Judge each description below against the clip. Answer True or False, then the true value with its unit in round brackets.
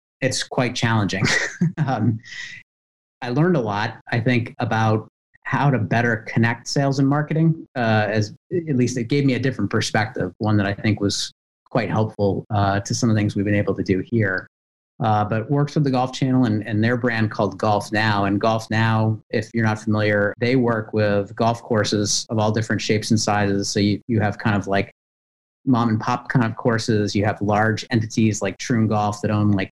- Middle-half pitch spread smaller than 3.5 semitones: True (2.9 semitones)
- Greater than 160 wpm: True (205 wpm)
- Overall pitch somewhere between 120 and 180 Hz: False (110 Hz)